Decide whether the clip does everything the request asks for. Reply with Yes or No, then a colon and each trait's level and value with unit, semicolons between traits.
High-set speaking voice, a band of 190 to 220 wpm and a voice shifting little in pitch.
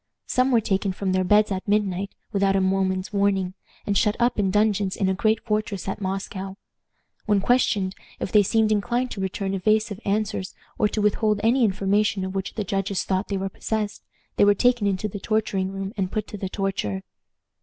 Yes: high, 200 Hz; average, 195 wpm; narrow, 1.8 semitones